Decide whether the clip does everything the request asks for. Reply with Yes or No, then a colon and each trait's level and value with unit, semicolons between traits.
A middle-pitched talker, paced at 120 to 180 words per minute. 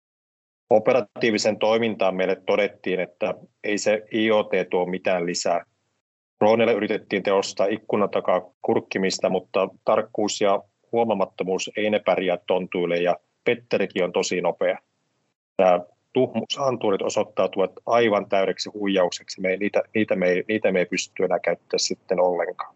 No: low, 100 Hz; average, 130 wpm